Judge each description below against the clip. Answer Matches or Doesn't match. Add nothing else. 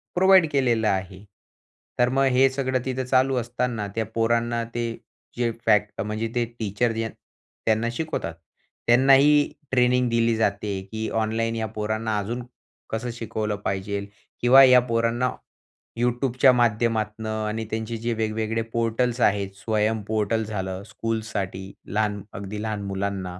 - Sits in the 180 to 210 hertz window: Doesn't match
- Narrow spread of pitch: Matches